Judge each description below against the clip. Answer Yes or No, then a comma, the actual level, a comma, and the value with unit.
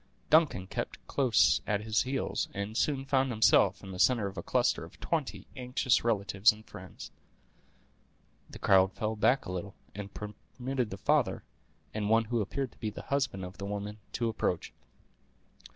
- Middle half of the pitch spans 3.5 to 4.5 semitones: Yes, average, 4.0 semitones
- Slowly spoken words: No, average, 170 wpm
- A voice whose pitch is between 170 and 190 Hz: No, low, 110 Hz